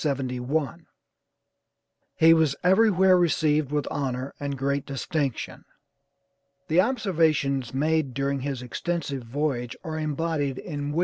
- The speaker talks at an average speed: No, slow, 110 wpm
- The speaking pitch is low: No, medium, 145 Hz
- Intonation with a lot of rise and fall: No, average, 3.0 semitones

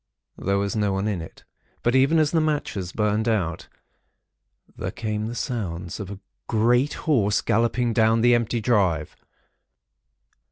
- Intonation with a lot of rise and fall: No, average, 3.5 semitones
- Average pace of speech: Yes, average, 150 wpm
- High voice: No, low, 110 Hz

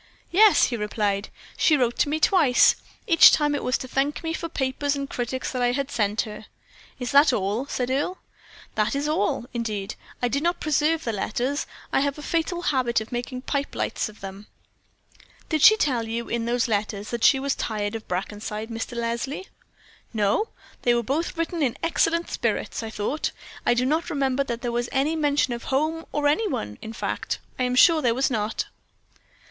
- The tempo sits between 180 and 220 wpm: Yes, average, 195 wpm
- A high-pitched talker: Yes, very high, 255 Hz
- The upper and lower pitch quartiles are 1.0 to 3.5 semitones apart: No, average, 4.6 semitones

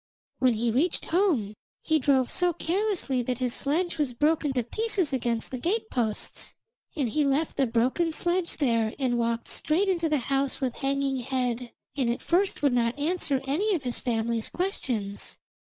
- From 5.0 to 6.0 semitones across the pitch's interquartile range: Yes, wide, 5.4 semitones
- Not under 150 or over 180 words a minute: Yes, average, 175 wpm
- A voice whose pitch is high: Yes, very high, 275 Hz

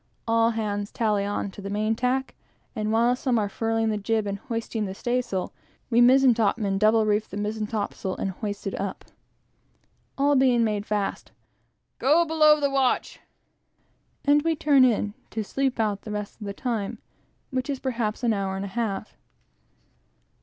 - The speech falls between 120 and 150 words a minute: No, average, 175 wpm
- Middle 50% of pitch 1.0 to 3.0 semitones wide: No, average, 3.5 semitones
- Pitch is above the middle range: Yes, high, 220 Hz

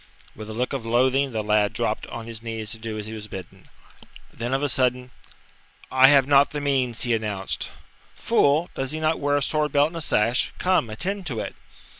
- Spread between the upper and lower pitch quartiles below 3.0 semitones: No, average, 4.3 semitones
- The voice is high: No, low, 125 Hz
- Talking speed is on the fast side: Yes, fast, 215 wpm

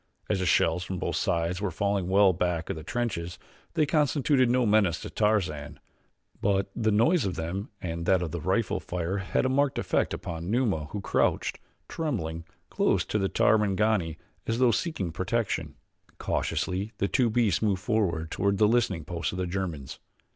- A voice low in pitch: Yes, very low, 95 Hz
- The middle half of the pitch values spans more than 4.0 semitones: Yes, average, 4.6 semitones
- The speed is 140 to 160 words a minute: No, average, 175 wpm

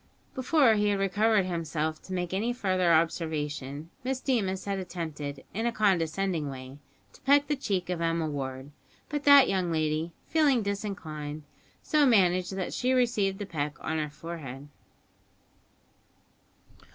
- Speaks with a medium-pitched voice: Yes, medium, 180 Hz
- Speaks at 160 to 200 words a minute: No, average, 145 wpm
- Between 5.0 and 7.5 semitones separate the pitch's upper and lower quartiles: Yes, wide, 5.5 semitones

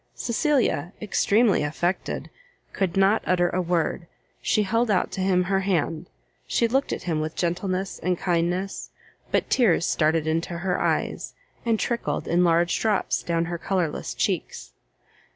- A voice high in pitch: No, medium, 180 Hz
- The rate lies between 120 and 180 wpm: Yes, average, 150 wpm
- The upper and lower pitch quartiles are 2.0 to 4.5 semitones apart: Yes, average, 2.8 semitones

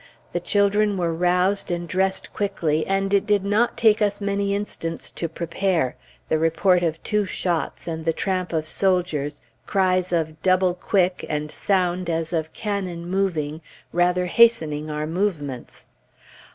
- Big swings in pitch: No, average, 3.3 semitones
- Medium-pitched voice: Yes, medium, 180 Hz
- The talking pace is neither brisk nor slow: Yes, average, 150 wpm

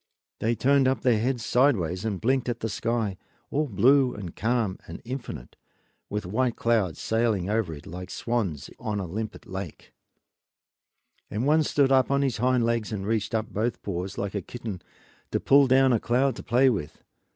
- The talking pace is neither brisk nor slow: Yes, average, 185 wpm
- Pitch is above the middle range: No, low, 115 Hz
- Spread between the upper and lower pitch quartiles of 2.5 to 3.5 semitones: No, average, 4.3 semitones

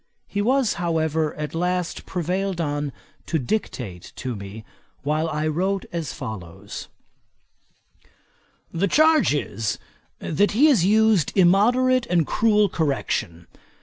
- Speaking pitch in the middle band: Yes, medium, 170 Hz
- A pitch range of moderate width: No, wide, 5.7 semitones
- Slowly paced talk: Yes, slow, 115 wpm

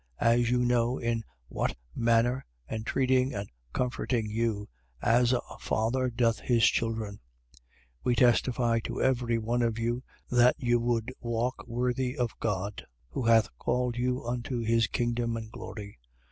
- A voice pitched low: Yes, low, 120 Hz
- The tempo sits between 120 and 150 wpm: Yes, average, 145 wpm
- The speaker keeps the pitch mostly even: Yes, narrow, 1.4 semitones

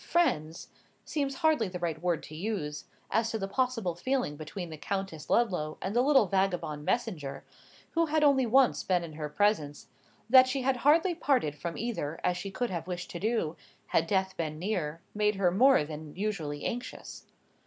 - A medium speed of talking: Yes, average, 180 wpm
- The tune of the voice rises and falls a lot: Yes, wide, 7.3 semitones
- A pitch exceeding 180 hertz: Yes, high, 190 Hz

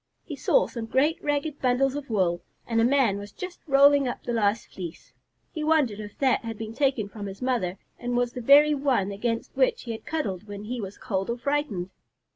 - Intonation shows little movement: No, wide, 5.4 semitones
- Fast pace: Yes, fast, 215 wpm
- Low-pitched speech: No, high, 240 Hz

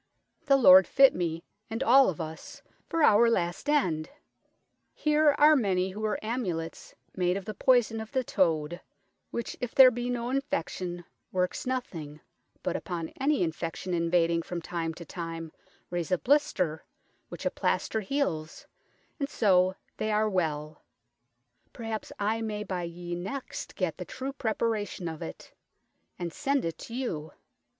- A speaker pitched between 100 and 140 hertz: No, high, 190 Hz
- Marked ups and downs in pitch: Yes, wide, 6.3 semitones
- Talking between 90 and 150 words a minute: No, average, 160 wpm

